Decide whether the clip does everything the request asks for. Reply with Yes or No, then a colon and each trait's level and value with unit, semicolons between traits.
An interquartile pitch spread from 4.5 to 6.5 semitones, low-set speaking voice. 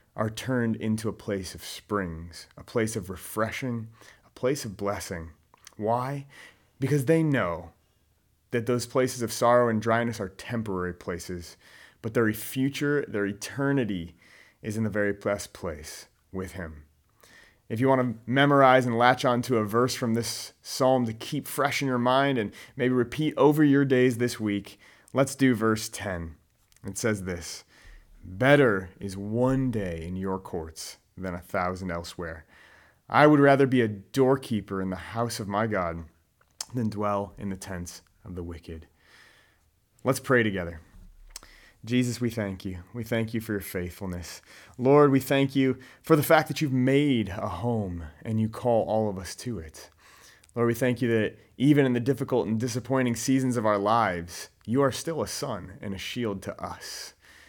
Yes: average, 5.0 semitones; low, 110 Hz